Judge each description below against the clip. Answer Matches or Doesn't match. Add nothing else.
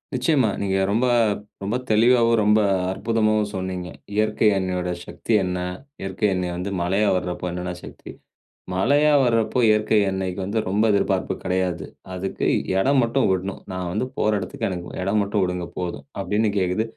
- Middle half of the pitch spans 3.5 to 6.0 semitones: Doesn't match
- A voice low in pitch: Matches